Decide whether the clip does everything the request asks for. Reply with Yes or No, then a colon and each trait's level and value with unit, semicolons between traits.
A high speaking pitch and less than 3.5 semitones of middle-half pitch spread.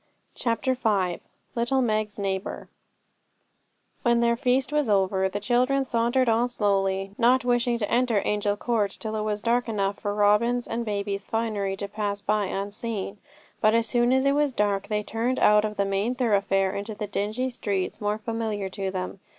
Yes: high, 215 Hz; average, 3.0 semitones